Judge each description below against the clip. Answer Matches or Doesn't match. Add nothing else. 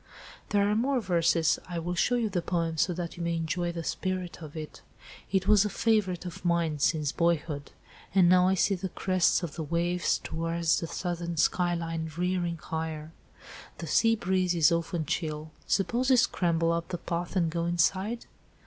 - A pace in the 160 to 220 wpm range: Matches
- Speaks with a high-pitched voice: Doesn't match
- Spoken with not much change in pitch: Matches